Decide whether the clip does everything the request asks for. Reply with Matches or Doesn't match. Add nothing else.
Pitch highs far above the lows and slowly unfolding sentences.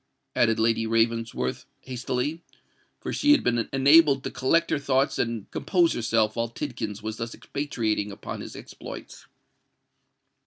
Doesn't match